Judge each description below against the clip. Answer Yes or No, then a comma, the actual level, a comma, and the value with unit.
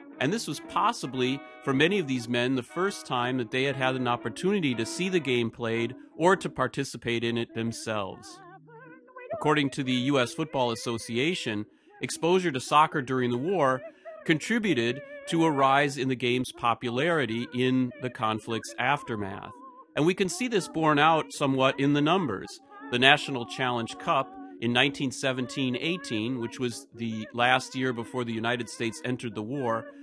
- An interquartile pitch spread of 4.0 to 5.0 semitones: Yes, average, 4.5 semitones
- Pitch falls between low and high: No, low, 130 Hz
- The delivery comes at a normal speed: Yes, average, 165 wpm